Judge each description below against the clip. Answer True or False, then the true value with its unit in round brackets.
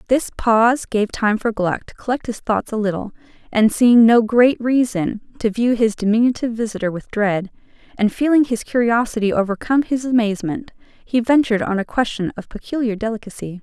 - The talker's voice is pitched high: True (225 Hz)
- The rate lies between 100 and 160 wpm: False (170 wpm)